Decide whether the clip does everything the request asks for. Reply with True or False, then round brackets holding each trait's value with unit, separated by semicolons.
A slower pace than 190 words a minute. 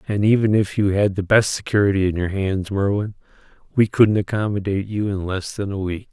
False (205 wpm)